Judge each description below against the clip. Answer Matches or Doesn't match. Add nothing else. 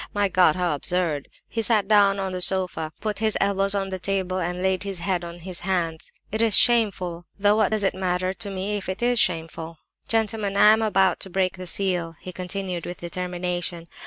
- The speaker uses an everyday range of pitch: Doesn't match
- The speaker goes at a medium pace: Doesn't match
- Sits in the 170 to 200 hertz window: Matches